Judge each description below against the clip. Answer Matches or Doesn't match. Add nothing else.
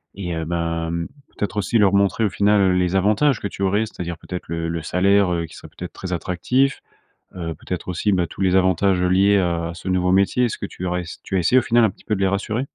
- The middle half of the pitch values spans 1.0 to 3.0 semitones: Matches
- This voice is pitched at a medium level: Doesn't match